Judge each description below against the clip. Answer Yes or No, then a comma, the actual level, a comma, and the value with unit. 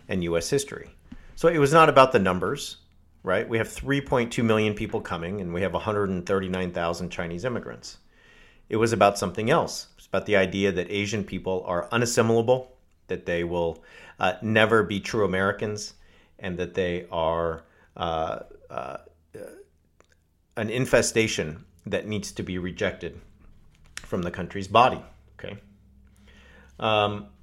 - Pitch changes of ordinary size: Yes, average, 4.0 semitones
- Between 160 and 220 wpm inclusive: No, average, 140 wpm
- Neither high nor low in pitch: No, very low, 95 Hz